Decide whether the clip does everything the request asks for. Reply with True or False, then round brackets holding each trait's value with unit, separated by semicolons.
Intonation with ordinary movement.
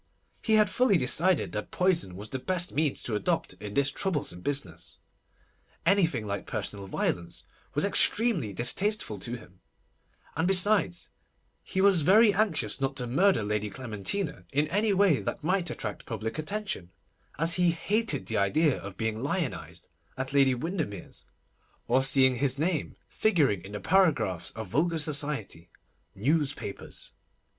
False (8.8 semitones)